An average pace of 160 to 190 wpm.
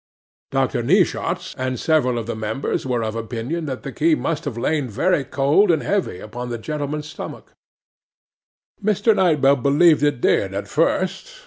Yes: average, 165 wpm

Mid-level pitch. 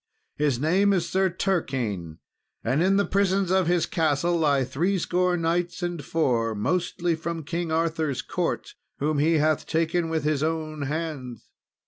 Yes: medium, 165 Hz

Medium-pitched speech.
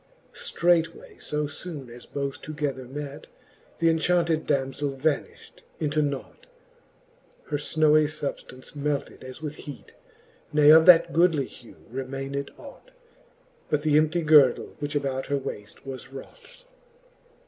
Yes: medium, 150 Hz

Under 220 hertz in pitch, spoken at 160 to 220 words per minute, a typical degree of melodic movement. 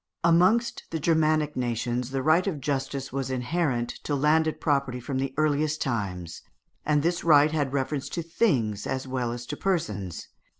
Yes: medium, 140 Hz; average, 165 wpm; average, 4.0 semitones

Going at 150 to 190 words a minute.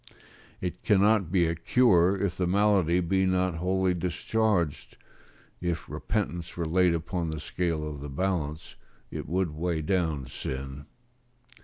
No: average, 140 wpm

